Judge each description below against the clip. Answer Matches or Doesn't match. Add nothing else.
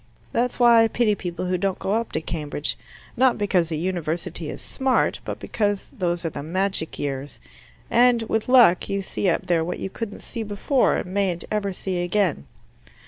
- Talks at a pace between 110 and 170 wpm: Doesn't match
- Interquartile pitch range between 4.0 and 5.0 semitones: Matches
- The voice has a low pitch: Doesn't match